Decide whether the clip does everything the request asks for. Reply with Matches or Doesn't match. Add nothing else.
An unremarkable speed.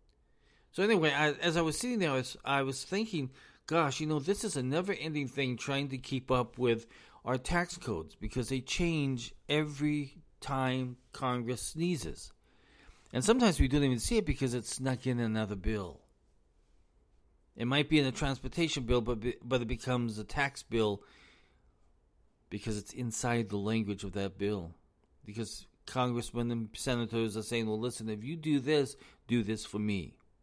Matches